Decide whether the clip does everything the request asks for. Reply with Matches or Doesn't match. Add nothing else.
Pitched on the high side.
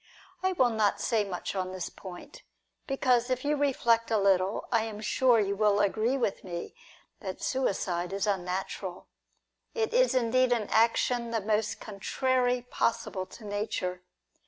Matches